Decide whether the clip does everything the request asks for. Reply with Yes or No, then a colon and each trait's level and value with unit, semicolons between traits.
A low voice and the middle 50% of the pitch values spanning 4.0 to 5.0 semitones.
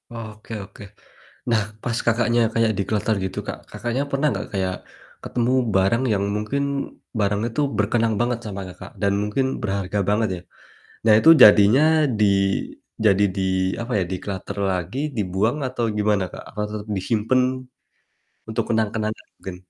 No: low, 105 Hz; narrow, 2.6 semitones